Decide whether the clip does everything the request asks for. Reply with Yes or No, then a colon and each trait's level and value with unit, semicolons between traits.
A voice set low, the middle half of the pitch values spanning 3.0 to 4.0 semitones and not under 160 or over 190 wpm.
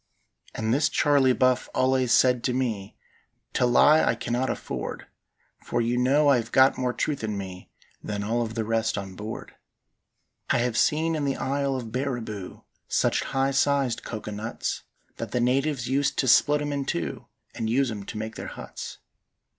Yes: low, 125 Hz; average, 3.5 semitones; average, 180 wpm